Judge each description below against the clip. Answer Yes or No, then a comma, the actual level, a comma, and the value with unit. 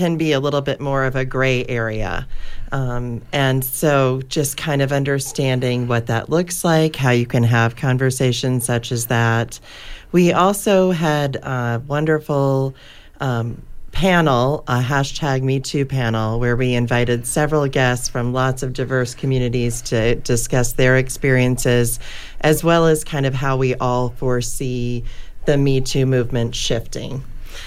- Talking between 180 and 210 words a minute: No, average, 150 wpm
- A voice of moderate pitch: No, low, 130 Hz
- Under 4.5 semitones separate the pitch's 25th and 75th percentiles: Yes, narrow, 2.6 semitones